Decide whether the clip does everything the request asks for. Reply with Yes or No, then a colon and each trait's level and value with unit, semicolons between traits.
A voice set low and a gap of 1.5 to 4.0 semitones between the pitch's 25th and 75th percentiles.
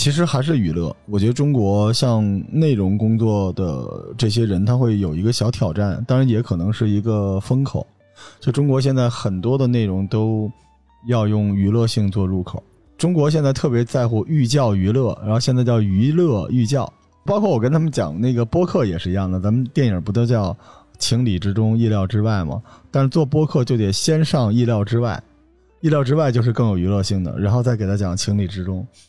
No: low, 115 Hz; average, 4.6 semitones